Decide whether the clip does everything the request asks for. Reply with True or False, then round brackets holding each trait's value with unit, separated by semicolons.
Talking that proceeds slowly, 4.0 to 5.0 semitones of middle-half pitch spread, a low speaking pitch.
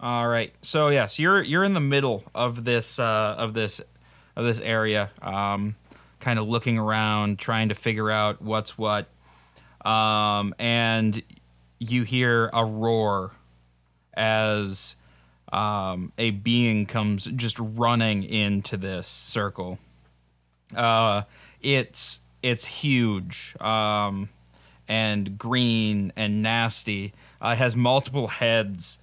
False (120 wpm; 3.0 semitones; 110 Hz)